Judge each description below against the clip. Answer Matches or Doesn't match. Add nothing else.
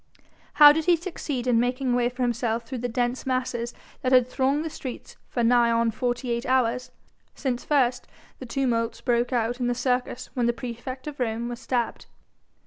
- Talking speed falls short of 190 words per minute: Doesn't match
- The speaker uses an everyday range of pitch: Doesn't match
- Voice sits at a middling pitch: Doesn't match